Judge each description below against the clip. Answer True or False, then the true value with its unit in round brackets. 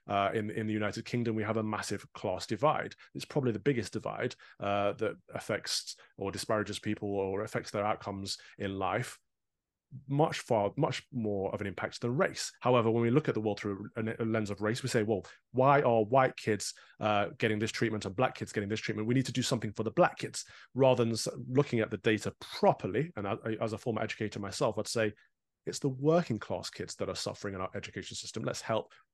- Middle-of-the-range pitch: False (110 Hz)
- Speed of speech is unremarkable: False (220 wpm)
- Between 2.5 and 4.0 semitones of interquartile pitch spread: True (2.9 semitones)